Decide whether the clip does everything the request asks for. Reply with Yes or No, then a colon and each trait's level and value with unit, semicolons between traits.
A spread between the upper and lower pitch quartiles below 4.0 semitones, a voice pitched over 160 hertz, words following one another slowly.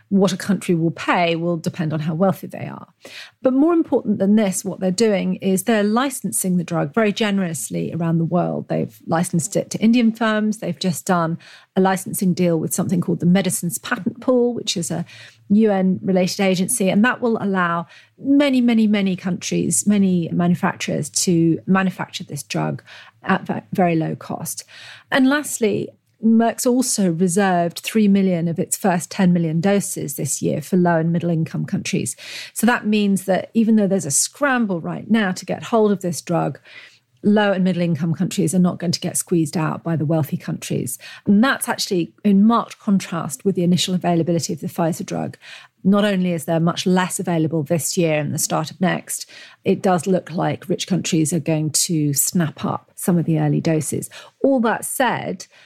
No: average, 3.3 semitones; medium, 185 Hz; average, 190 wpm